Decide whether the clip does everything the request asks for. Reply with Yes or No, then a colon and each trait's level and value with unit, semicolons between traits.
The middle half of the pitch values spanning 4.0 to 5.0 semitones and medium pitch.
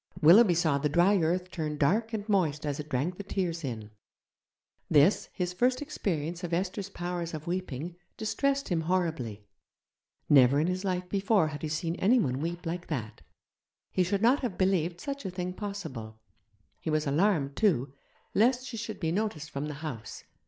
Yes: average, 4.6 semitones; medium, 175 Hz